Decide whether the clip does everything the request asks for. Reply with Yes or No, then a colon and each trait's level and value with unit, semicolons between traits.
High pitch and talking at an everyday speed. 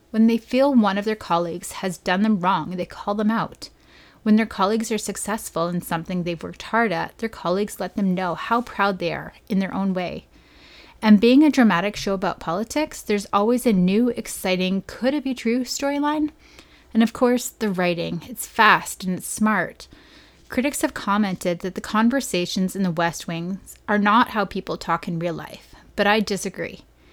Yes: high, 205 Hz; average, 190 wpm